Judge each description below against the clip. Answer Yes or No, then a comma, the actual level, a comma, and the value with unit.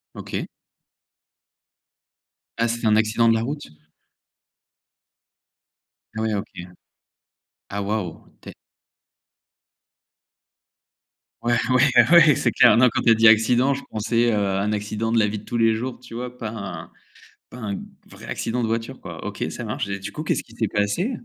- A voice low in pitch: Yes, low, 115 Hz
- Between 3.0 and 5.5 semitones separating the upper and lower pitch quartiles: No, narrow, 2.5 semitones